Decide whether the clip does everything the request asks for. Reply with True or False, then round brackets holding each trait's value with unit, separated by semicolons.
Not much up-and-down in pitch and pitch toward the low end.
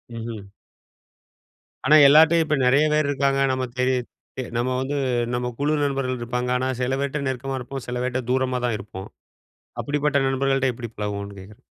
True (2.1 semitones; 130 Hz)